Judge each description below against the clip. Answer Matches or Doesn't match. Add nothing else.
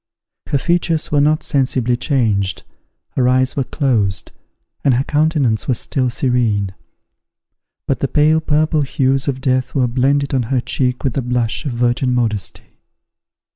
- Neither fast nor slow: Matches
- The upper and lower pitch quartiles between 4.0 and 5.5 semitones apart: Doesn't match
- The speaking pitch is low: Matches